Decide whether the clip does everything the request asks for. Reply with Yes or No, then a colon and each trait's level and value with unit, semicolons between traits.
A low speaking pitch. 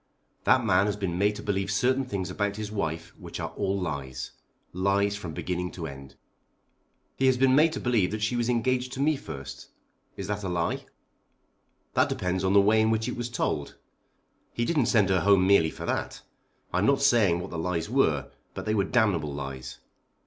Yes: low, 100 Hz